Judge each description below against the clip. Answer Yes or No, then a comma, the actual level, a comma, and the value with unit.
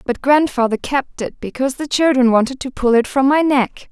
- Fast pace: Yes, fast, 215 wpm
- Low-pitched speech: No, very high, 260 Hz